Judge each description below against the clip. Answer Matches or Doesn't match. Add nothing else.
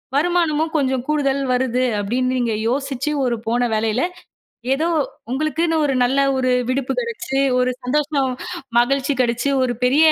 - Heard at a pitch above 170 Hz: Matches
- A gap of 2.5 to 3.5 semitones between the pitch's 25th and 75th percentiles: Matches